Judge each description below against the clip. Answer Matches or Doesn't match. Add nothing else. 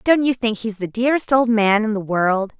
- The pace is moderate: Doesn't match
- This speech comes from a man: Doesn't match